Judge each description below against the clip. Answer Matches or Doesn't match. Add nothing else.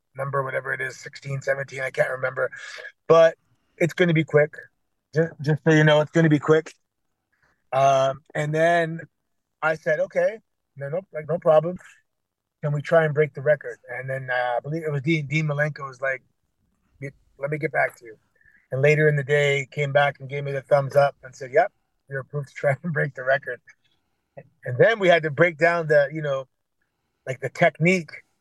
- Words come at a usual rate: Doesn't match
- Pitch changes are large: Doesn't match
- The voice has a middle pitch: Matches